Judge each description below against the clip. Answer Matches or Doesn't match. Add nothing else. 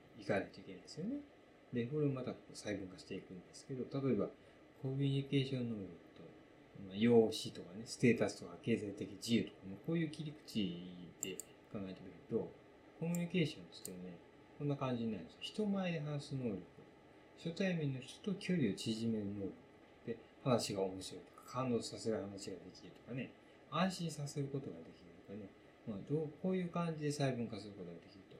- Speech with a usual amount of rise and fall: Doesn't match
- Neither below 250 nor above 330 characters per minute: Doesn't match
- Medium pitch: Doesn't match